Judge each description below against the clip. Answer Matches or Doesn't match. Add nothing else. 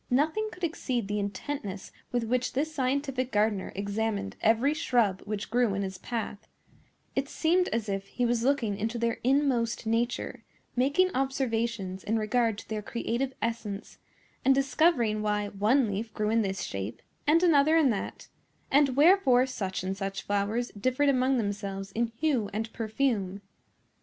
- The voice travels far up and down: Doesn't match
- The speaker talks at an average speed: Matches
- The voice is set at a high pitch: Matches